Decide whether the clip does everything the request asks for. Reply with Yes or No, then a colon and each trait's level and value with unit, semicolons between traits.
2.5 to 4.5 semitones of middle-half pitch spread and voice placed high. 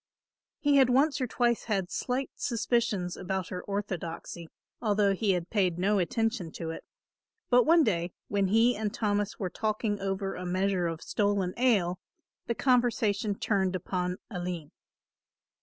Yes: average, 4.0 semitones; high, 200 Hz